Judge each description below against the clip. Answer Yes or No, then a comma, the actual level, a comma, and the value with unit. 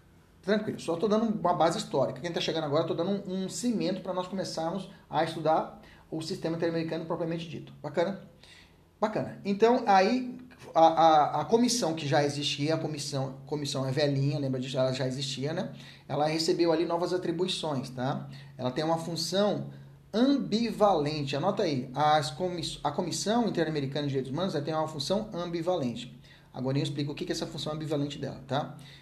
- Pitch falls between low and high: Yes, medium, 160 Hz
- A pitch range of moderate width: Yes, average, 4.0 semitones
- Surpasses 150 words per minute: Yes, average, 180 wpm